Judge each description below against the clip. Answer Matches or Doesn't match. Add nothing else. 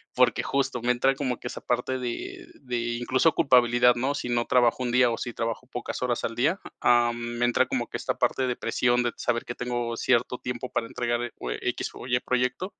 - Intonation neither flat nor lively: Doesn't match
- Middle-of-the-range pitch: Doesn't match